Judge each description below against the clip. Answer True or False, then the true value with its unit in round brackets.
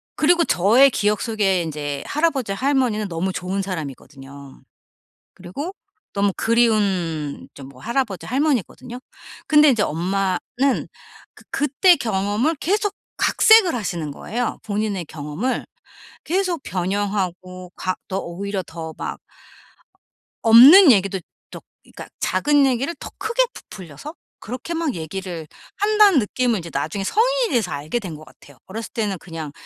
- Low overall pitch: False (205 Hz)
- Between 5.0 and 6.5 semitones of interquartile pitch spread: False (7.4 semitones)